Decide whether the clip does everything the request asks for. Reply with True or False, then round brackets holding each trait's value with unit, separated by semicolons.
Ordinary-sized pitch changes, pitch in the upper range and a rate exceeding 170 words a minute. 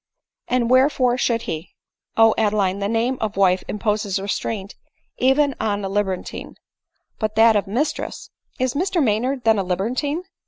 True (4.1 semitones; 220 Hz; 180 wpm)